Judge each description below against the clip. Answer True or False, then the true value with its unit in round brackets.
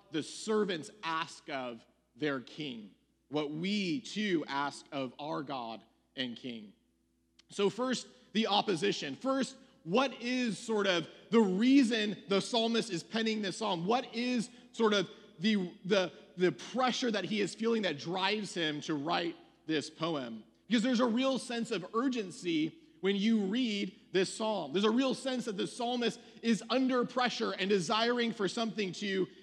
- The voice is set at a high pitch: True (210 Hz)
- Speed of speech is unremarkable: True (160 wpm)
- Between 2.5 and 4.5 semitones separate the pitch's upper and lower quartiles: False (5.6 semitones)